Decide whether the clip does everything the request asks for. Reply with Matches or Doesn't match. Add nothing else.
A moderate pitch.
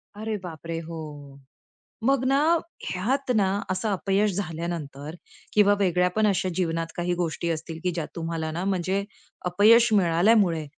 Matches